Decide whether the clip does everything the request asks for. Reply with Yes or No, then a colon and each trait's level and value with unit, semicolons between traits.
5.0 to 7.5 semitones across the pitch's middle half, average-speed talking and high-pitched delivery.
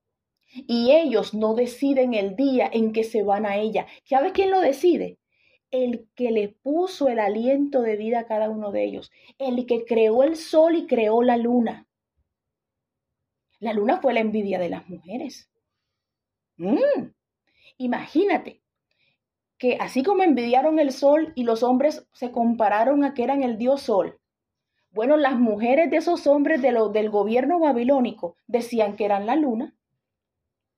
No: average, 4.4 semitones; average, 160 wpm; high, 245 Hz